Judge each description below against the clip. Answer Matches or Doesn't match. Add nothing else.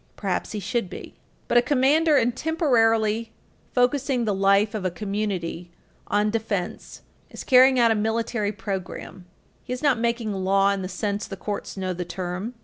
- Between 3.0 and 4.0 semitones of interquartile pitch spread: Matches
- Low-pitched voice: Doesn't match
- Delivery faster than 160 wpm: Matches